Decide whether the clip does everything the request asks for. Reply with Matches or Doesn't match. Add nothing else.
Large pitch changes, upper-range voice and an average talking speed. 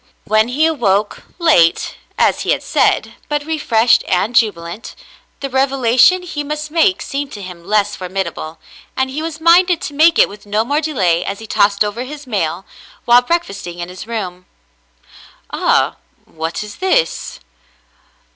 Matches